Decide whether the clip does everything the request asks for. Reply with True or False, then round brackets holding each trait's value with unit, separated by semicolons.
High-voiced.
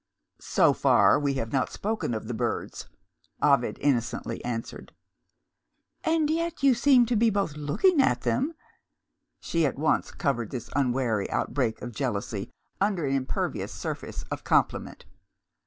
False (145 Hz)